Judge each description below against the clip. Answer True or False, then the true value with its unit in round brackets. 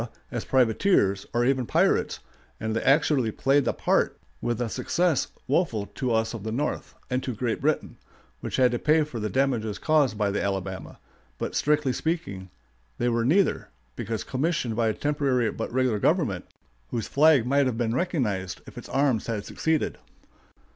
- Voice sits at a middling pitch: False (125 Hz)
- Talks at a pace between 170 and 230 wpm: True (175 wpm)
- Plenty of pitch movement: False (4.5 semitones)